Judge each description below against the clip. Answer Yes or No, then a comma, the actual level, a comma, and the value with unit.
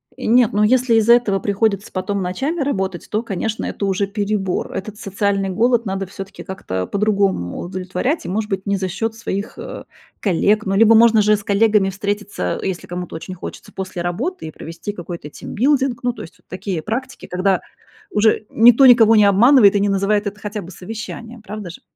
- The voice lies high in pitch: Yes, high, 205 Hz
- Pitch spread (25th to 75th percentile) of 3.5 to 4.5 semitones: No, average, 2.8 semitones